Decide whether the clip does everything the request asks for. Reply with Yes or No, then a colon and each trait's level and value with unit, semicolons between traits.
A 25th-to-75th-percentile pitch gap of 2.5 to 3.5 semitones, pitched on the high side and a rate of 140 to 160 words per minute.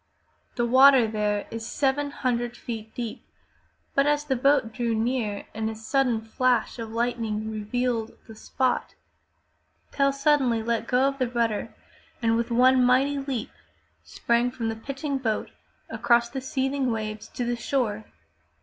Yes: average, 2.9 semitones; high, 240 Hz; average, 150 wpm